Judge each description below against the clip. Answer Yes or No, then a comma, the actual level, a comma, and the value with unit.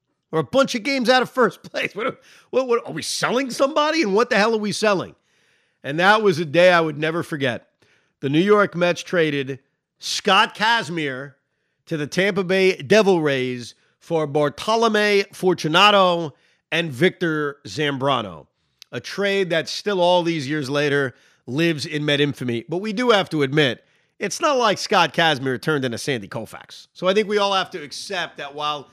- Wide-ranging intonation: Yes, wide, 5.7 semitones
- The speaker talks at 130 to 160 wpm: No, average, 185 wpm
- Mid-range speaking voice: Yes, medium, 165 Hz